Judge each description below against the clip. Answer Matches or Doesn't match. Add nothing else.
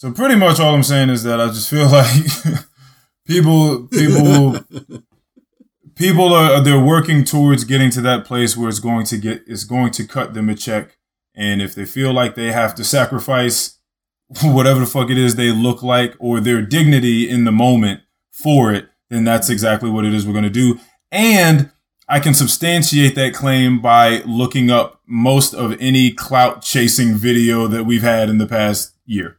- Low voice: Matches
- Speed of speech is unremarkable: Matches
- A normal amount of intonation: Matches